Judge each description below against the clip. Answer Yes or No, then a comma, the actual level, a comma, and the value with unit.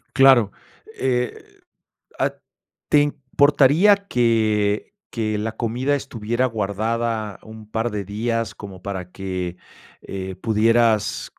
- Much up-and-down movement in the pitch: No, average, 3.3 semitones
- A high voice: No, low, 115 Hz